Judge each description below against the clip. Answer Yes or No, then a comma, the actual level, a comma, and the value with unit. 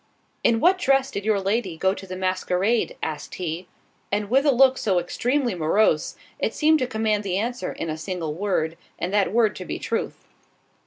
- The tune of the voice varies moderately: Yes, average, 4.8 semitones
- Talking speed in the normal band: Yes, average, 195 wpm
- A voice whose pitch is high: Yes, high, 205 Hz